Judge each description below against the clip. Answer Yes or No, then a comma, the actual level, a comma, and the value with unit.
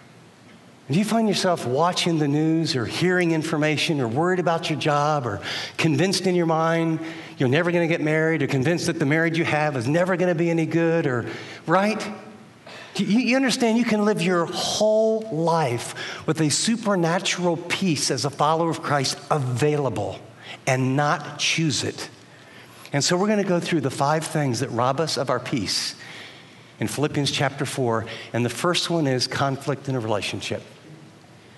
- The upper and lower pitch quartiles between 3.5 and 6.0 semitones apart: Yes, average, 4.1 semitones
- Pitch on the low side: No, medium, 160 Hz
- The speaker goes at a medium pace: Yes, average, 180 wpm